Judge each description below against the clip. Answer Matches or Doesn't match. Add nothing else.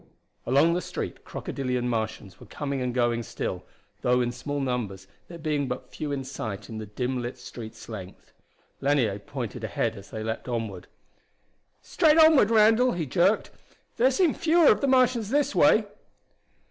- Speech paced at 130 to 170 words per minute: Matches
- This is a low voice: Matches